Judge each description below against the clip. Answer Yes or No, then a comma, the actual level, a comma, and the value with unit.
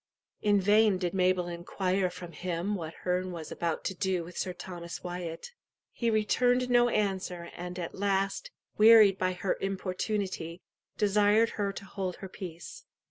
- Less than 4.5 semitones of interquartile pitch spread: Yes, narrow, 2.5 semitones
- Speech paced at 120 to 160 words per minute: Yes, average, 155 wpm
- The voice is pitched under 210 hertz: Yes, medium, 185 Hz